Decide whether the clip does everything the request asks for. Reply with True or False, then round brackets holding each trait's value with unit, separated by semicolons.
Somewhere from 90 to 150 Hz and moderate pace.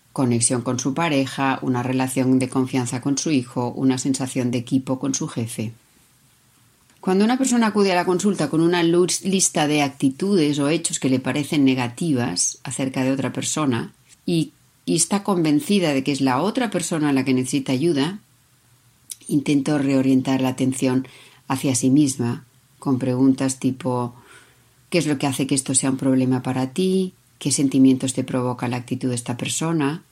True (135 Hz; 175 wpm)